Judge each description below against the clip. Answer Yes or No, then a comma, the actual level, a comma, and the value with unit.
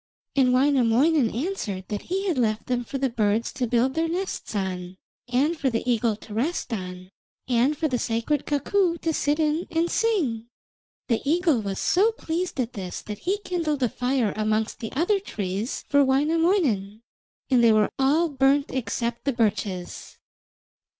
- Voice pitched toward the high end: Yes, very high, 255 Hz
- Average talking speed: Yes, average, 170 wpm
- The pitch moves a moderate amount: No, wide, 6.3 semitones